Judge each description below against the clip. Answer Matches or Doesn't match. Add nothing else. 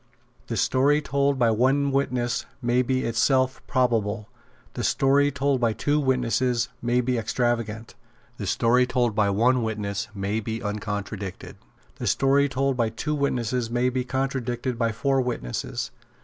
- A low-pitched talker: Matches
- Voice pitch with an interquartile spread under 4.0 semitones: Matches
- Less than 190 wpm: Matches